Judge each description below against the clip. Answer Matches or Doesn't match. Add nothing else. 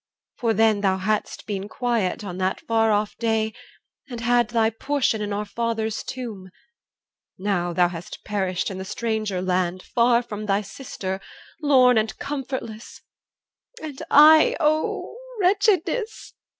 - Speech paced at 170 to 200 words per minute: Doesn't match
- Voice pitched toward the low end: Doesn't match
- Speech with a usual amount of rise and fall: Matches